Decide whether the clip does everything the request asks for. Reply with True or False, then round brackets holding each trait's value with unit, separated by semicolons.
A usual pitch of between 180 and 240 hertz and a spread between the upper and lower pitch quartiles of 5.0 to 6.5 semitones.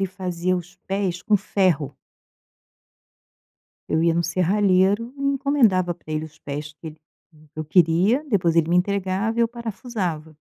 False (185 Hz; 3.8 semitones)